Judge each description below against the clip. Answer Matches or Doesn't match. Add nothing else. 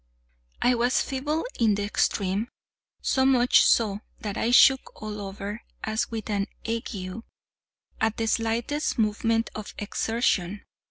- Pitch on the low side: Doesn't match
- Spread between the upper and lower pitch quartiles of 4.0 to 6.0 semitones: Doesn't match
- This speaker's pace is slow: Matches